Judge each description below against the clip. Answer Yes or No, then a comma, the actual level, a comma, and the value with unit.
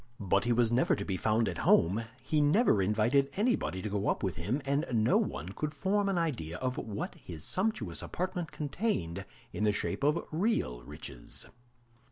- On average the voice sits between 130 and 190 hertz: No, low, 115 Hz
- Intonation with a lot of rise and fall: Yes, wide, 8.2 semitones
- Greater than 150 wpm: Yes, average, 185 wpm